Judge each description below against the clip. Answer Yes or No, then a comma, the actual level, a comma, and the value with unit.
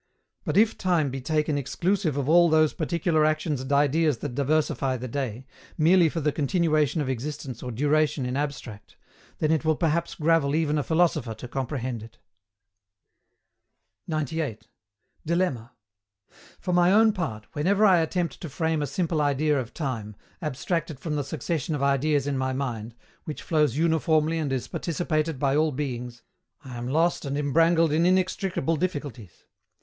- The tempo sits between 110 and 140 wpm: No, average, 160 wpm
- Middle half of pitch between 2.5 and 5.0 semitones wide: Yes, average, 3.6 semitones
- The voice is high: No, medium, 150 Hz